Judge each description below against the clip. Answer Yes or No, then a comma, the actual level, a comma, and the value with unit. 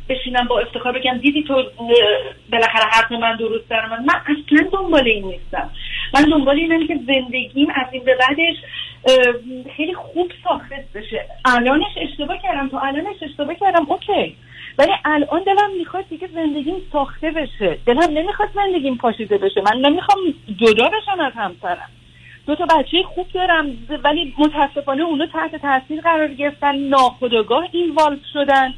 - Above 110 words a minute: Yes, average, 150 wpm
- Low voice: No, very high, 290 Hz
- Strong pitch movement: No, average, 4.4 semitones